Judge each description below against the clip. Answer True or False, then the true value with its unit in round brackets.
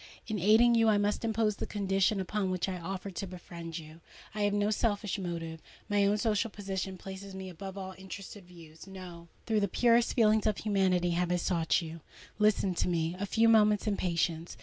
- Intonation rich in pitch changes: False (3.0 semitones)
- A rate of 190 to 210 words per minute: True (195 wpm)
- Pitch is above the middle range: True (195 Hz)